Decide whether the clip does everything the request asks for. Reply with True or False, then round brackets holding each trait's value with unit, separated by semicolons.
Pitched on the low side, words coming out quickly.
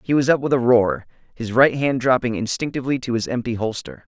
True (125 Hz; 215 wpm)